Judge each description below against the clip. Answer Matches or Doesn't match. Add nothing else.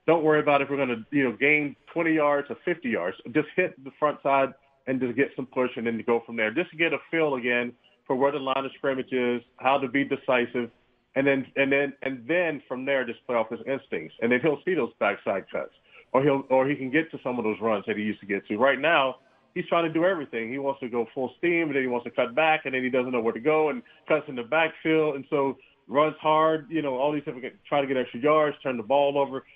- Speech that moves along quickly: Matches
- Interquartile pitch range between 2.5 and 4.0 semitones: Matches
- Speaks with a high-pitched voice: Doesn't match